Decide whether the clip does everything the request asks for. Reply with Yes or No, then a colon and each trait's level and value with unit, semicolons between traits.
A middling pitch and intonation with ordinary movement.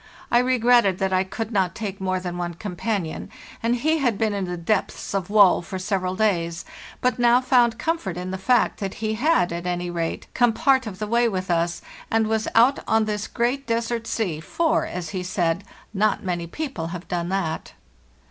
No: high, 200 Hz; average, 4.6 semitones